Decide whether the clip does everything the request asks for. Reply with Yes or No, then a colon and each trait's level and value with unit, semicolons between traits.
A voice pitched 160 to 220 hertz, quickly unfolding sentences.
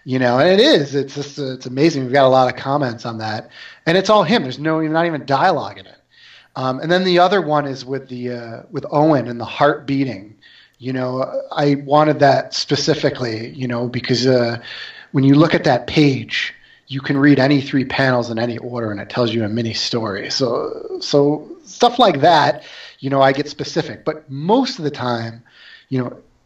No: low, 135 Hz; fast, 215 wpm